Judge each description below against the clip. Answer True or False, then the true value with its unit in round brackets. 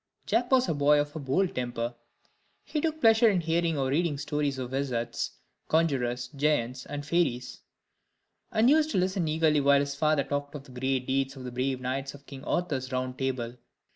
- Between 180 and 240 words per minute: True (190 wpm)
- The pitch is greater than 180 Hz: False (140 Hz)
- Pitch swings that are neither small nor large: True (3.9 semitones)